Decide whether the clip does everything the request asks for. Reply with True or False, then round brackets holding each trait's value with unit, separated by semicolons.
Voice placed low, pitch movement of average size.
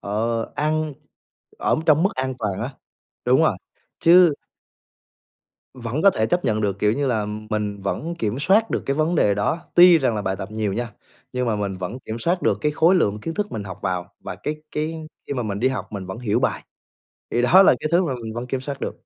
False (125 Hz; 6.8 semitones)